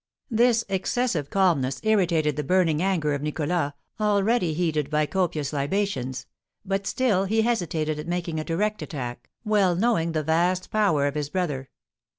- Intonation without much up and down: No, average, 4.7 semitones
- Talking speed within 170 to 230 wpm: No, average, 155 wpm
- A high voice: No, medium, 170 Hz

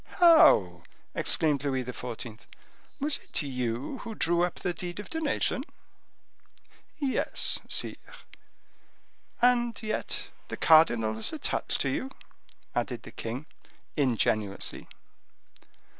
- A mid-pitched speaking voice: Yes, medium, 155 Hz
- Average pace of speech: No, slow, 105 wpm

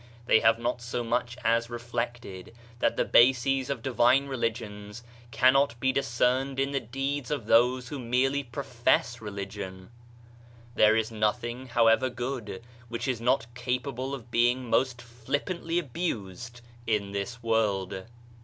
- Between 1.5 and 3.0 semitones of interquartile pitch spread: Yes, narrow, 2.5 semitones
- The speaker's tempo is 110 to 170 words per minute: Yes, average, 140 wpm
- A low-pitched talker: Yes, low, 120 Hz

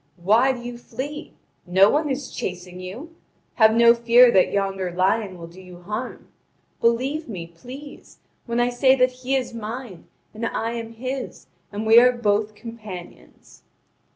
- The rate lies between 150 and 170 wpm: Yes, average, 160 wpm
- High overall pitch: Yes, high, 230 Hz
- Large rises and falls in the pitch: No, average, 4.5 semitones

